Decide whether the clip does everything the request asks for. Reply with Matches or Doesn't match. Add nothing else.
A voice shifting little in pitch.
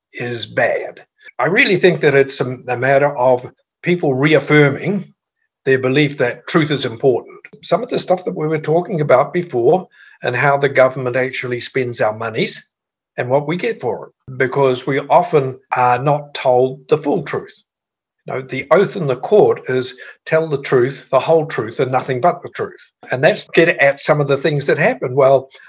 Doesn't match